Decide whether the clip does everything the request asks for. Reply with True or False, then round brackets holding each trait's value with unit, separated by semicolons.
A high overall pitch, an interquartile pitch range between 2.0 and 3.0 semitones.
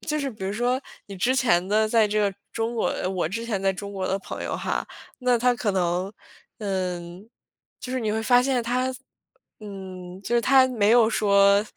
False (210 Hz; 3.9 semitones)